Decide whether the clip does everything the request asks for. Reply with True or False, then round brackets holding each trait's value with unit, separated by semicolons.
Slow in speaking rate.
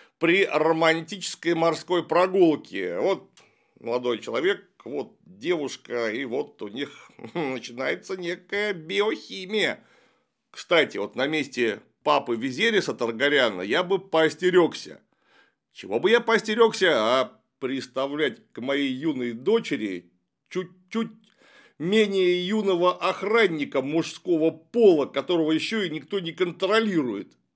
True (105 wpm)